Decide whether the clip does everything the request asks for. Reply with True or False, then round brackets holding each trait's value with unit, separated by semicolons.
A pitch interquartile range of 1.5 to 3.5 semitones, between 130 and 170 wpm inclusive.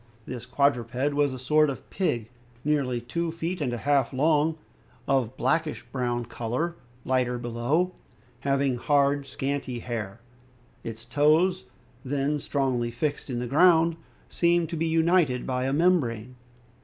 False (4.1 semitones; 145 wpm)